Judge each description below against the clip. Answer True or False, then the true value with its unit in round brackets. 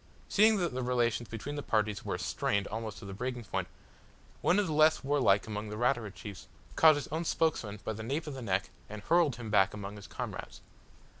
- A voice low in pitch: True (115 Hz)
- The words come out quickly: True (215 wpm)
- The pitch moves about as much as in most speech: False (5.8 semitones)